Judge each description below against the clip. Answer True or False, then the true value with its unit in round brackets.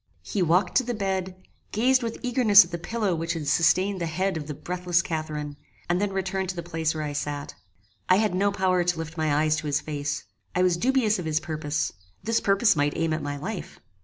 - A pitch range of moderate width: True (3.9 semitones)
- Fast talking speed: True (225 wpm)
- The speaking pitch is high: False (175 Hz)